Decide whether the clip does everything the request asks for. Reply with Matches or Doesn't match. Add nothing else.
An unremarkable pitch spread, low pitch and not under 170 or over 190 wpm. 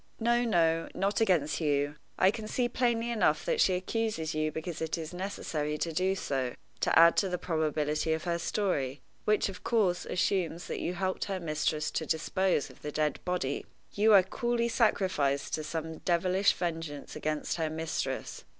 Doesn't match